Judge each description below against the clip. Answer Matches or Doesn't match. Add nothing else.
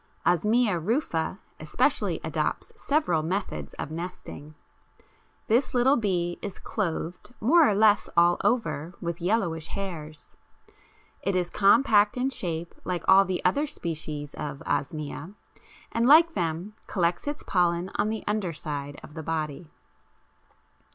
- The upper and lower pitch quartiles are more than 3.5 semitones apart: Matches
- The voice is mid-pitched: Matches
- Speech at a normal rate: Doesn't match